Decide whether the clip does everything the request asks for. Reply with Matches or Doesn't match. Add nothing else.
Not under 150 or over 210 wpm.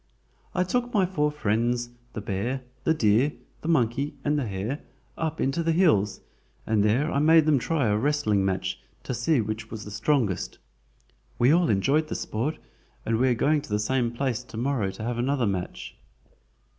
Matches